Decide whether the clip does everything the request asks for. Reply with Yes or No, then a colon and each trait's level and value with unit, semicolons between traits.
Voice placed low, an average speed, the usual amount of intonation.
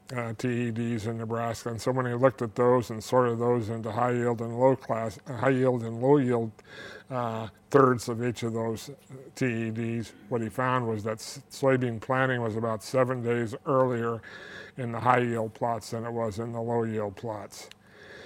No: low, 120 Hz; average, 185 wpm; narrow, 1.9 semitones